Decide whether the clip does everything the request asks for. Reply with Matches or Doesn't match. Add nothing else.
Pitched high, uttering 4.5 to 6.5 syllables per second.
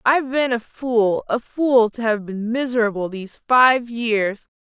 Doesn't match